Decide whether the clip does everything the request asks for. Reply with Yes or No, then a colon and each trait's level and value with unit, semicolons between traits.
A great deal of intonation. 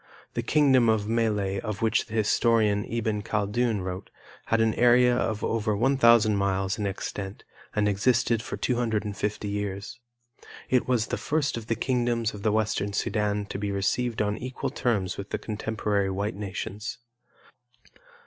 No: narrow, 2.4 semitones